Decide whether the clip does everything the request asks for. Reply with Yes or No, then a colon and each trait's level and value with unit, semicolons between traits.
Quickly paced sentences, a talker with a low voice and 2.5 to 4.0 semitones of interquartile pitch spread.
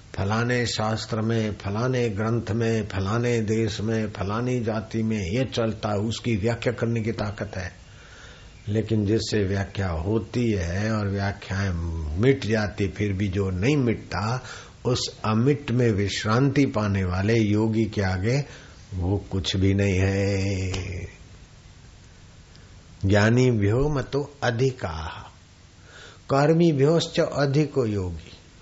No: average, 115 wpm; low, 105 Hz; average, 3.2 semitones